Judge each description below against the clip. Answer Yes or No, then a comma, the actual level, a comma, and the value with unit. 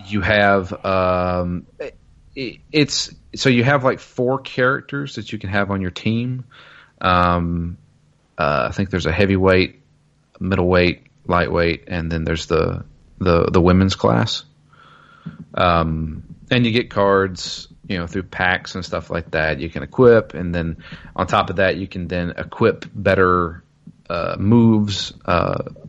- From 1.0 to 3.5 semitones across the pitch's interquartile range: No, average, 4.0 semitones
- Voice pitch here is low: Yes, very low, 95 Hz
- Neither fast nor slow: Yes, average, 150 wpm